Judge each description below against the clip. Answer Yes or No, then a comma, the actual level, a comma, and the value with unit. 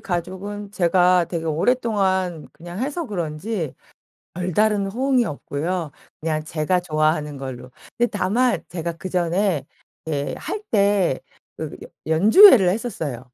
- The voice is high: No, medium, 180 Hz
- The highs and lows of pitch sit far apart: No, average, 4.7 semitones